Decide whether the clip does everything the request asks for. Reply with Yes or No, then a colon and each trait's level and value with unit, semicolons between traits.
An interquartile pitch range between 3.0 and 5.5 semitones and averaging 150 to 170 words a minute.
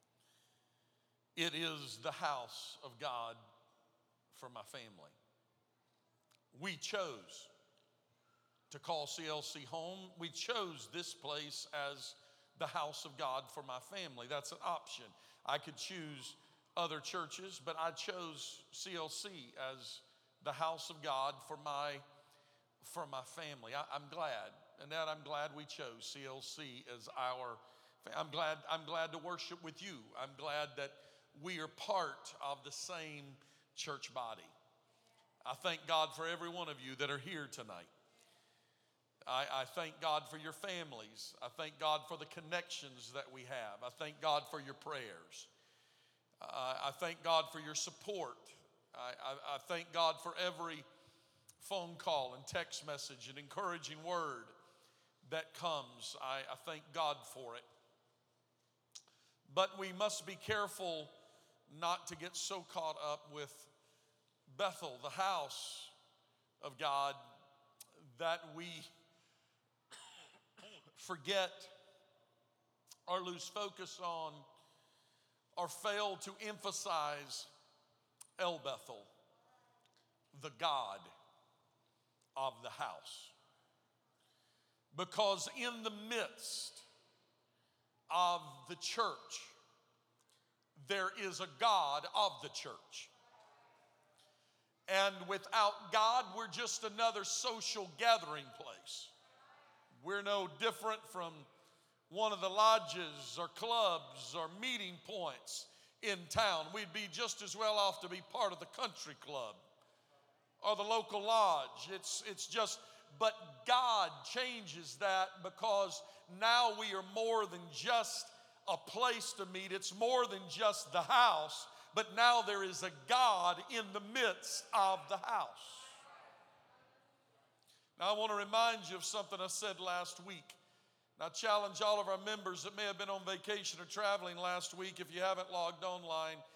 No: average, 5.2 semitones; slow, 135 wpm